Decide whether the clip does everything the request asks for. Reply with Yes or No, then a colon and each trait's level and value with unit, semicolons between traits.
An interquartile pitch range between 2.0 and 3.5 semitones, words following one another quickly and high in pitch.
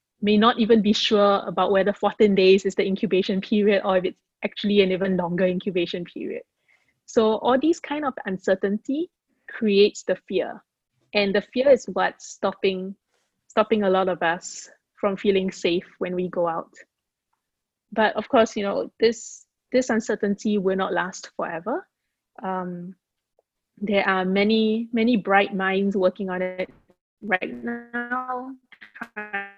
No: average, 2.9 semitones; average, 150 wpm; high, 205 Hz